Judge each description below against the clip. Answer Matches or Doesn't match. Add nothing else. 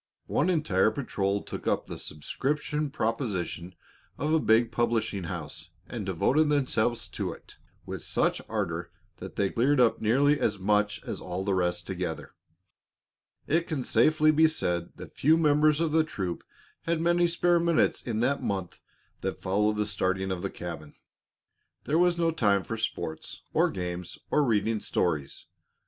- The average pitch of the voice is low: Matches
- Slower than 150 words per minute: Doesn't match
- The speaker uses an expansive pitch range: Matches